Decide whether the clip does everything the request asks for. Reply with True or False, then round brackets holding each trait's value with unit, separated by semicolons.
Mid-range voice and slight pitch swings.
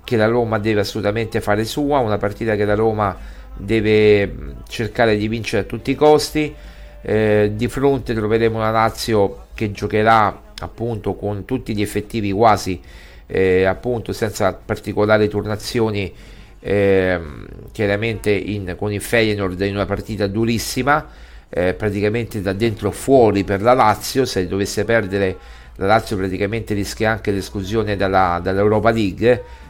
False (105 Hz; 2.3 semitones)